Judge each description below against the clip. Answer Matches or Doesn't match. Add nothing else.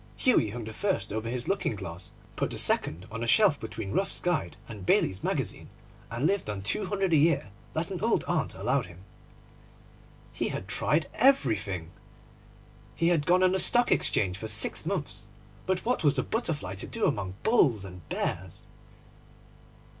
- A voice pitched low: Matches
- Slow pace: Doesn't match